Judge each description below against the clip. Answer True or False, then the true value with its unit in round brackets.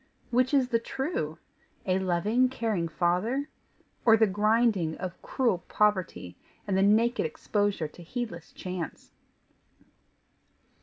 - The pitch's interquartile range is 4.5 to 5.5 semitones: True (5.2 semitones)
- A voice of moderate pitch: False (205 Hz)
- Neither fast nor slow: False (115 wpm)